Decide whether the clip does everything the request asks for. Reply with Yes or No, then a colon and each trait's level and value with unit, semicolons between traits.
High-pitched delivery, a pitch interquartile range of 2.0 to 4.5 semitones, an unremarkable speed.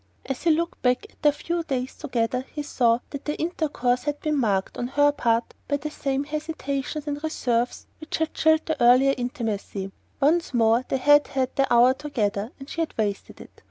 Yes: very high, 275 Hz; average, 3.8 semitones; average, 195 wpm